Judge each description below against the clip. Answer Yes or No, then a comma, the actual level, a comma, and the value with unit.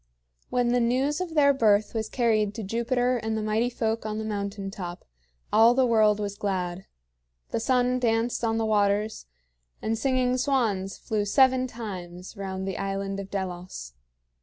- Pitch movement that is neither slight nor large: Yes, average, 3.6 semitones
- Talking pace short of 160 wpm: No, average, 165 wpm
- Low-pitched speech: No, high, 220 Hz